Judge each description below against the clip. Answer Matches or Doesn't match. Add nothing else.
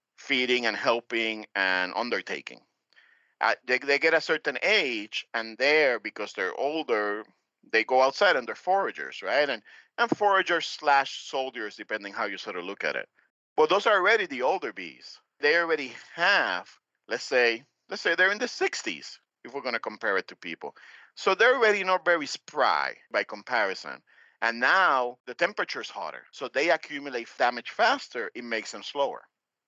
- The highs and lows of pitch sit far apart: Matches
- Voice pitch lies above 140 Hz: Doesn't match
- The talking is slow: Doesn't match